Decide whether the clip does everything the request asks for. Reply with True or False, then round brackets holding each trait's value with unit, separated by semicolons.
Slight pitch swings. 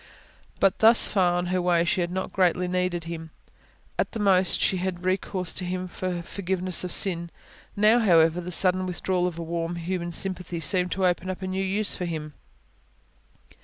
True (1.4 semitones)